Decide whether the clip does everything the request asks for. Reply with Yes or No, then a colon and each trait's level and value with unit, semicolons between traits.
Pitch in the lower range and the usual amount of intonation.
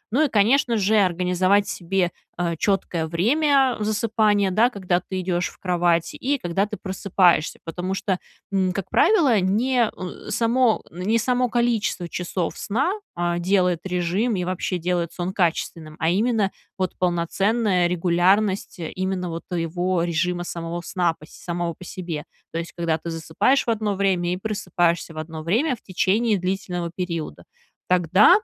No: medium, 185 Hz; average, 3.4 semitones